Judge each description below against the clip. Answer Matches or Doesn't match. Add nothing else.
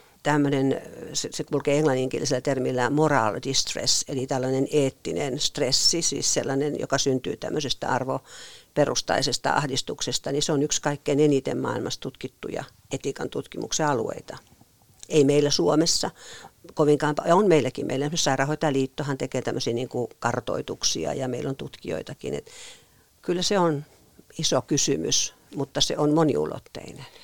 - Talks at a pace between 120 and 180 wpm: Matches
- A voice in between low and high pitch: Matches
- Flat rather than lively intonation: Matches